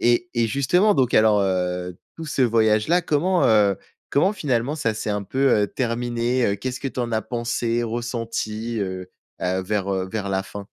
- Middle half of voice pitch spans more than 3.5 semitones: Yes, average, 3.9 semitones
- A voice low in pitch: Yes, low, 115 Hz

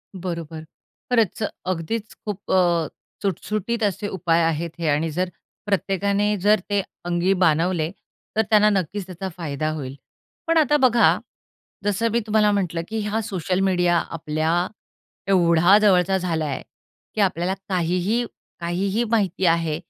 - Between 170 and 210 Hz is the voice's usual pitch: Yes, medium, 185 Hz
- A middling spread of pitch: Yes, average, 3.7 semitones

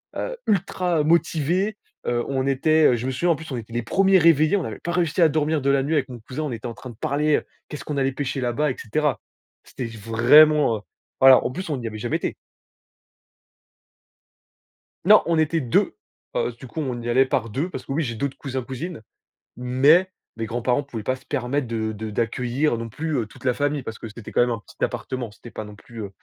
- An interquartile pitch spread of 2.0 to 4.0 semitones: No, average, 4.6 semitones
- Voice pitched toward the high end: No, low, 135 Hz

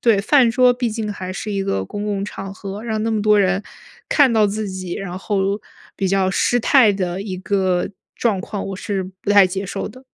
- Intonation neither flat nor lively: No, narrow, 2.2 semitones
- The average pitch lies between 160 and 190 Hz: No, high, 200 Hz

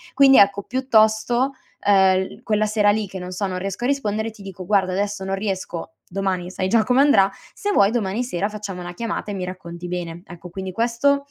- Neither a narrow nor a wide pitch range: Yes, average, 3.2 semitones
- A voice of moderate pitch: No, high, 200 Hz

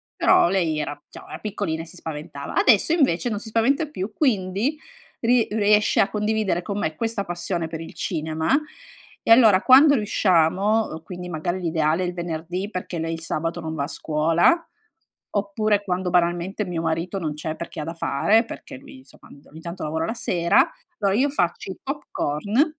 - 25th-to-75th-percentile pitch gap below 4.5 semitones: No, average, 5.0 semitones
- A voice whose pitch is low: No, medium, 185 Hz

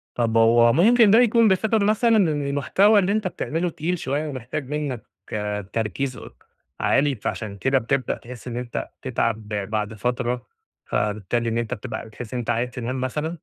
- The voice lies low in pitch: Yes, low, 130 Hz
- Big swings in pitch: Yes, wide, 5.9 semitones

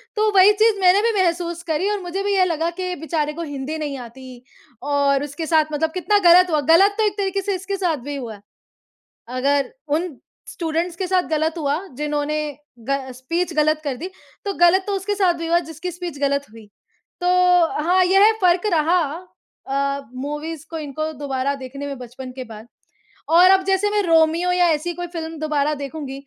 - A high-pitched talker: Yes, very high, 325 Hz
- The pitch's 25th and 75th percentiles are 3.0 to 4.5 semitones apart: Yes, average, 4.2 semitones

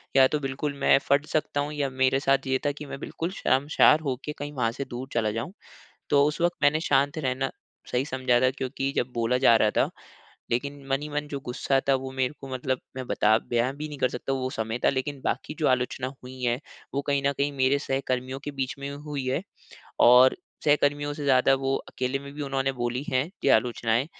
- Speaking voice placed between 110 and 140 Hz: Yes, low, 135 Hz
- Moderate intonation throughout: No, narrow, 1.9 semitones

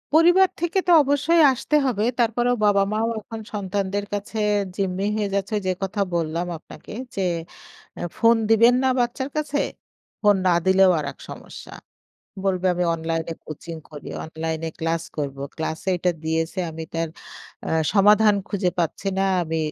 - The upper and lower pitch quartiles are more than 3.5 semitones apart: Yes, average, 5.3 semitones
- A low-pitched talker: No, high, 195 Hz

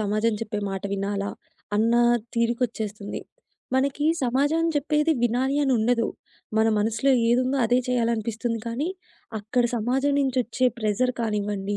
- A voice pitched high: Yes, high, 235 Hz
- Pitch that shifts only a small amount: No, average, 3.5 semitones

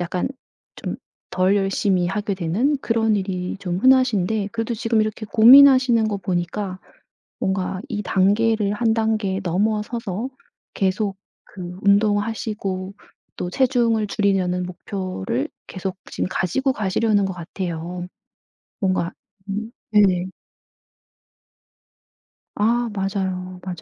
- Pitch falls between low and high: No, high, 200 Hz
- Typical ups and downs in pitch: Yes, average, 3.1 semitones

